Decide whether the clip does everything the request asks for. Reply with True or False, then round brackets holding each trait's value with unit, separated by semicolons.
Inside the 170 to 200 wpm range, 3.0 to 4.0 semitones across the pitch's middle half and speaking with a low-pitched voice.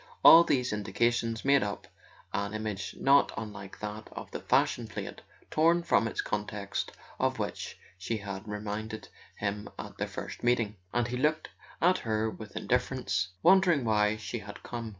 False (160 wpm; 3.3 semitones; 110 Hz)